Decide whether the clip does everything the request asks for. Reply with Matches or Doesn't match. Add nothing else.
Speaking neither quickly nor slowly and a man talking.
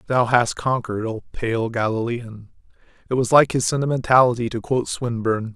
Matches